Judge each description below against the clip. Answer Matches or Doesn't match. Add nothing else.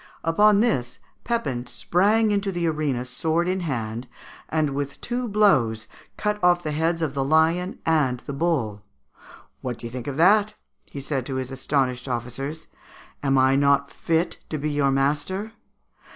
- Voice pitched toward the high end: Doesn't match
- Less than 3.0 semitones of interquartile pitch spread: Doesn't match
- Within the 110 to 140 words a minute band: Doesn't match